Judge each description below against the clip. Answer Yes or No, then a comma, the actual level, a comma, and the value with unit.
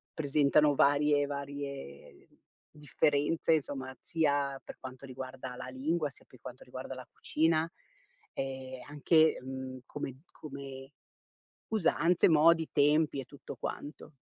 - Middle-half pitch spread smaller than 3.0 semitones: Yes, narrow, 2.5 semitones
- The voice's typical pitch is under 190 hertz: Yes, medium, 140 Hz